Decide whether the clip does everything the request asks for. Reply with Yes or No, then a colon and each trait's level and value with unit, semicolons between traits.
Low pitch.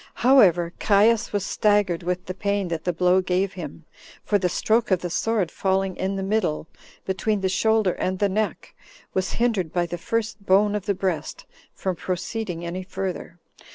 No: high, 190 Hz